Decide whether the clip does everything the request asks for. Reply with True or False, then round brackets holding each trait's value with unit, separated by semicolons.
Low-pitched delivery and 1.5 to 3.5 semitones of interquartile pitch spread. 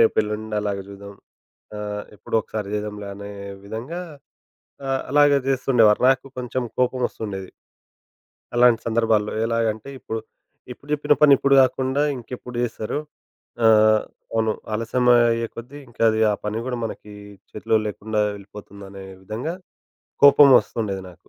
True (110 Hz; 3.1 semitones)